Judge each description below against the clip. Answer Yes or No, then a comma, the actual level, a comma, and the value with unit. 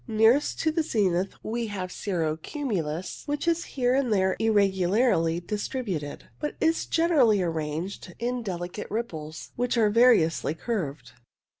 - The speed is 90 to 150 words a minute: Yes, average, 145 wpm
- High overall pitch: Yes, high, 210 Hz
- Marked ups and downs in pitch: Yes, wide, 6.2 semitones